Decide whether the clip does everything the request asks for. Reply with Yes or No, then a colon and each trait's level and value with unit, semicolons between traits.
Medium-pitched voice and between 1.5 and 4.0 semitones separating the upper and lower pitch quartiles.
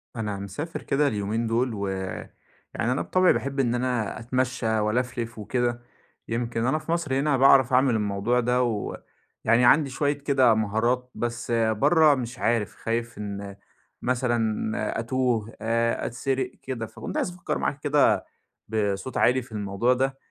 No: low, 120 Hz; average, 2.9 semitones